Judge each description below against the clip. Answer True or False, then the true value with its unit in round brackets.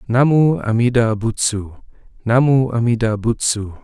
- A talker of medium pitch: False (115 Hz)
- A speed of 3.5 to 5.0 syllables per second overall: True (4.4 syllables/s)